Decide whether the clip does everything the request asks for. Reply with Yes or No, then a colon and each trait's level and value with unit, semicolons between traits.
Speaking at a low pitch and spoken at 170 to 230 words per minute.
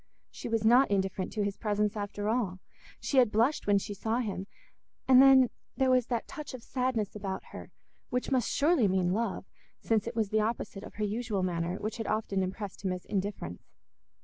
No: high, 215 Hz; average, 200 wpm